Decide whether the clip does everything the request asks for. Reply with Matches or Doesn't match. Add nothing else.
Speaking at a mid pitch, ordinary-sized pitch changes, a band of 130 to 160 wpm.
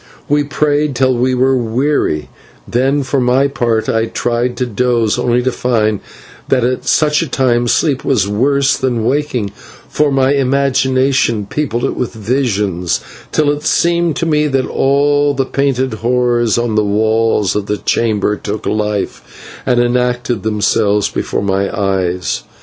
Doesn't match